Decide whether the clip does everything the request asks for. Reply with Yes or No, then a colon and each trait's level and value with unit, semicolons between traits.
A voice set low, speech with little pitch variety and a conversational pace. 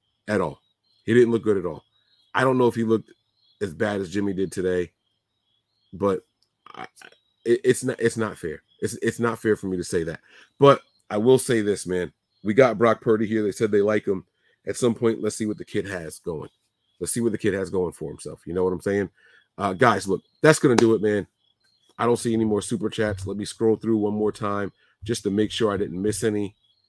No: low, 105 Hz; narrow, 2.3 semitones; fast, 240 wpm